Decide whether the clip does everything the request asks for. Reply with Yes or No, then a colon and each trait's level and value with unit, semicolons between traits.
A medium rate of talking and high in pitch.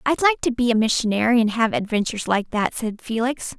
No: fast, 220 wpm; high, 230 Hz